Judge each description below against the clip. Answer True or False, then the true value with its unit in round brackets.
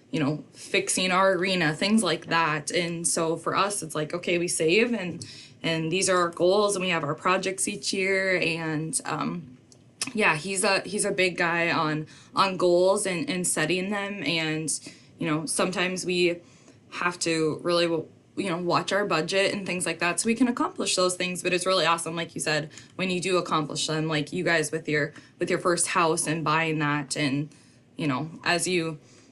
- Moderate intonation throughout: True (3.0 semitones)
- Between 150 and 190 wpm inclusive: False (200 wpm)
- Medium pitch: True (170 Hz)